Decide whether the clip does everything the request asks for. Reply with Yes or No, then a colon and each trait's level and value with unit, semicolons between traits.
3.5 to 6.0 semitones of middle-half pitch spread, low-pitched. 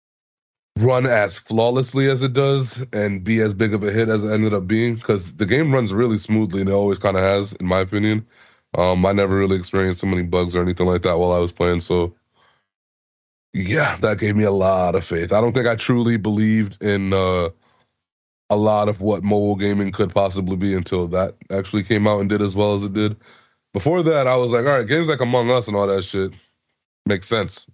No: average, 2.8 semitones; low, 105 Hz